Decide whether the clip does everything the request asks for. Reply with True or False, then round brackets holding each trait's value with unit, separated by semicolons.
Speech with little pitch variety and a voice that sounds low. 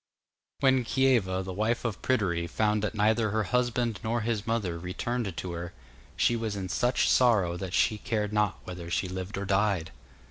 False (3.9 semitones; 105 Hz)